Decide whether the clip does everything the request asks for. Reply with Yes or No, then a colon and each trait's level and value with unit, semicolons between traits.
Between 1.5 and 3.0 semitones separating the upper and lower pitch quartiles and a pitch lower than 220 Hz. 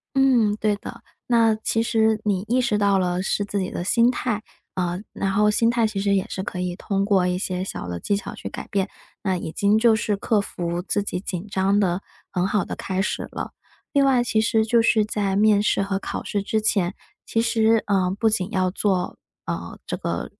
Yes: average, 2.7 semitones; high, 205 Hz